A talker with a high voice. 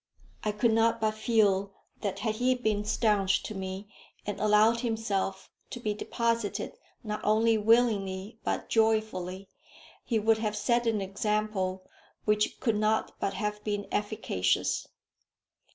Yes: high, 215 Hz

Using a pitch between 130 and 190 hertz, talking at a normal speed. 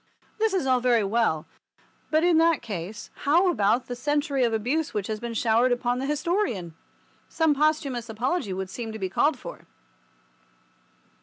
No: high, 245 Hz; average, 165 wpm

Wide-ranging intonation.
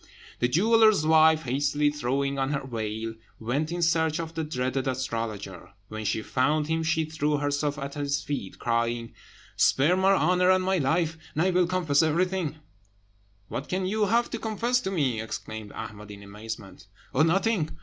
Yes: wide, 5.9 semitones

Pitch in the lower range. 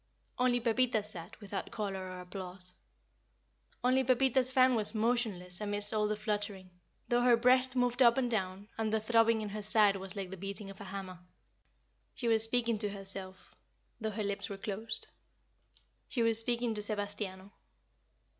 No: high, 215 Hz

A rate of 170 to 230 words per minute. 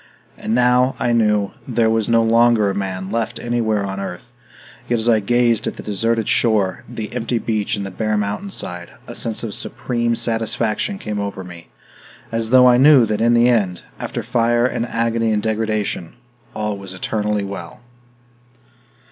Yes: average, 175 wpm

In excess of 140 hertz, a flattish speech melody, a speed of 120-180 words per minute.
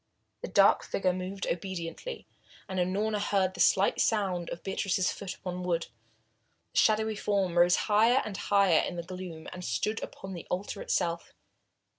Yes: medium, 185 Hz; narrow, 2.3 semitones; average, 165 wpm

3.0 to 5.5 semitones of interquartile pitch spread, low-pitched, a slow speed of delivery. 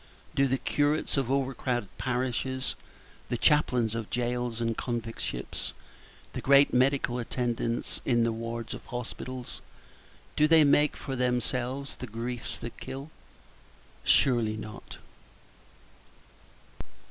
No: narrow, 2.4 semitones; low, 125 Hz; slow, 120 wpm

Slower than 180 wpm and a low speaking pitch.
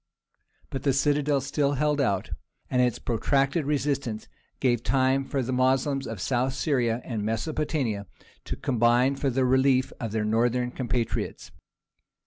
Yes: average, 140 wpm; low, 130 Hz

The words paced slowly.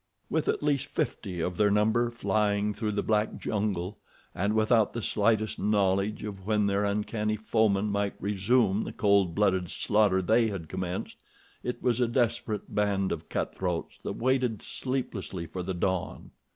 No: average, 165 wpm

